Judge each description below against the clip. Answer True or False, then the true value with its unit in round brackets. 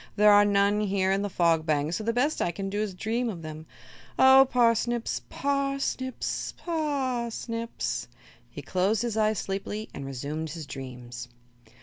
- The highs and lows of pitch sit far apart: True (6.1 semitones)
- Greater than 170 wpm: True (180 wpm)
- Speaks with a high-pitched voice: True (205 Hz)